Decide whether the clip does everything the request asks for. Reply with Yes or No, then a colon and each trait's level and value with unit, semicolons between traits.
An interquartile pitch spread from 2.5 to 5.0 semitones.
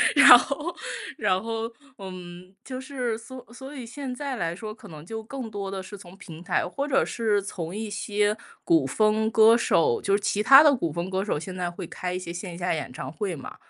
No: wide, 5.5 semitones